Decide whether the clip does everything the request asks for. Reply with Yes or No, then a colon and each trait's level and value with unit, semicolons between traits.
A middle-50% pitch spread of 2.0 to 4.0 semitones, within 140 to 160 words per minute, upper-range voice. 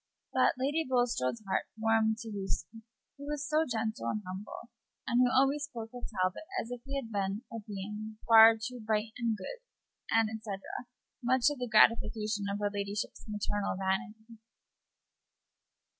Yes: average, 2.8 semitones; average, 155 wpm; high, 220 Hz